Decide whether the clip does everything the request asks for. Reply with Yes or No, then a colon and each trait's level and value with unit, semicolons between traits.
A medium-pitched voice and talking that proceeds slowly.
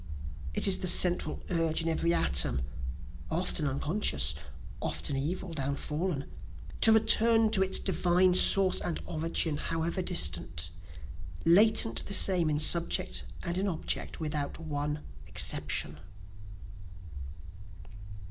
Yes: medium, 165 Hz; slow, 110 wpm